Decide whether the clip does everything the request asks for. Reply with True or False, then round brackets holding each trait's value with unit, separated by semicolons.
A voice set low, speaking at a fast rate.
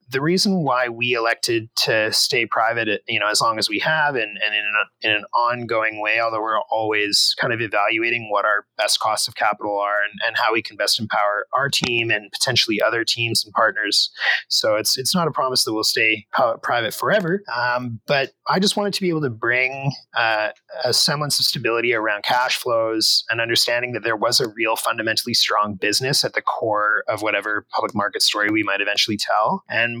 True (115 Hz; 210 wpm)